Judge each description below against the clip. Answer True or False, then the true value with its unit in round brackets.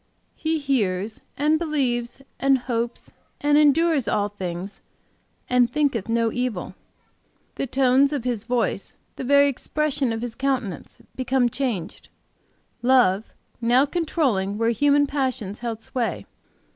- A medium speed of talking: False (125 wpm)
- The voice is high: True (250 Hz)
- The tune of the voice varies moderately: True (3.8 semitones)